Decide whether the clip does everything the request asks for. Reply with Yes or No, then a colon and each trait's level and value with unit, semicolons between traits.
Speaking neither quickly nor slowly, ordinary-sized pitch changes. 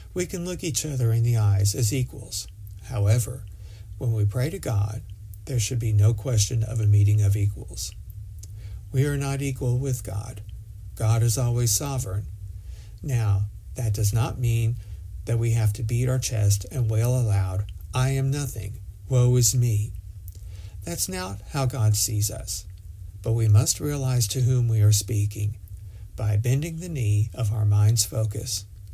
Yes: average, 165 wpm; average, 3.2 semitones